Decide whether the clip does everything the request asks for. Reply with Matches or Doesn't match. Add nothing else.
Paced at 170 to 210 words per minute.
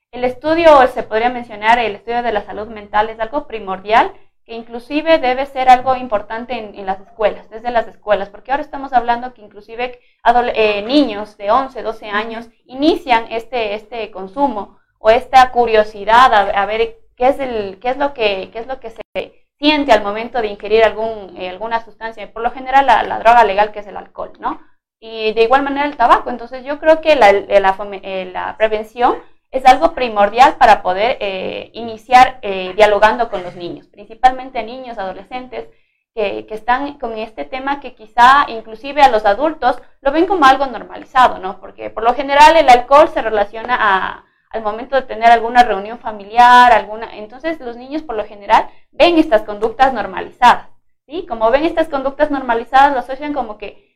Matches